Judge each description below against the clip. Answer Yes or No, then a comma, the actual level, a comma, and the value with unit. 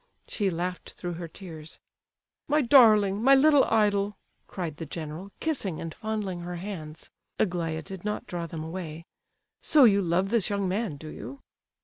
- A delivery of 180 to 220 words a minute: No, average, 160 wpm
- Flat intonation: No, average, 4.2 semitones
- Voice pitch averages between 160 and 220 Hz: Yes, medium, 185 Hz